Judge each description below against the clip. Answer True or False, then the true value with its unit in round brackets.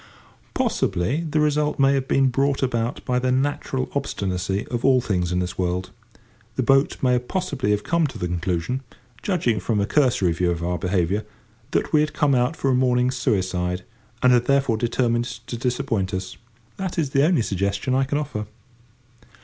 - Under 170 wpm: False (180 wpm)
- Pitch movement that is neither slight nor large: False (6.2 semitones)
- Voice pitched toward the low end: True (125 Hz)